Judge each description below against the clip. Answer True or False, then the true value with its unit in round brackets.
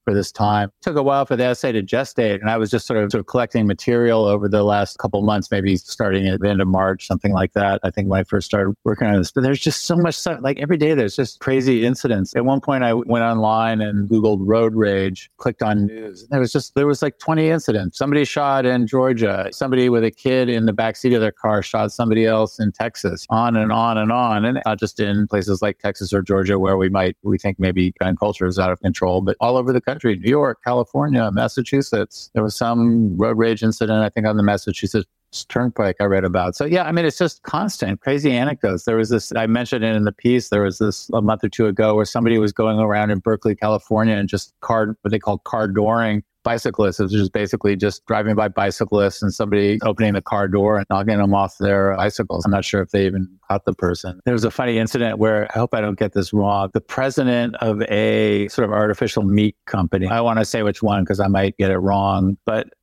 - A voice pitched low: True (110 Hz)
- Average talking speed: False (245 wpm)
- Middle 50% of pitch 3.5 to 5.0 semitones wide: False (2.9 semitones)